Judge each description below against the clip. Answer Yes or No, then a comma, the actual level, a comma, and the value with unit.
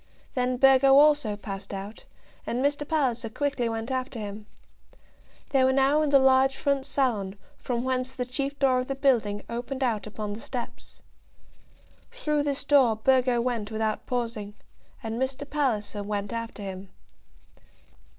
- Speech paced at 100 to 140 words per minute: No, average, 150 wpm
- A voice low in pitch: No, very high, 250 Hz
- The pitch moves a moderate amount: Yes, average, 3.8 semitones